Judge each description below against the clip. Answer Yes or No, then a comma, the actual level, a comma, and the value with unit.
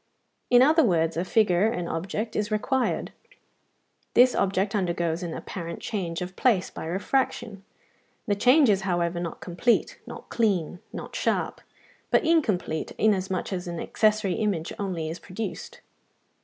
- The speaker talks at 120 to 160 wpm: Yes, average, 140 wpm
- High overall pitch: Yes, high, 195 Hz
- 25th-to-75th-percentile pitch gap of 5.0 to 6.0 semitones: No, average, 4.1 semitones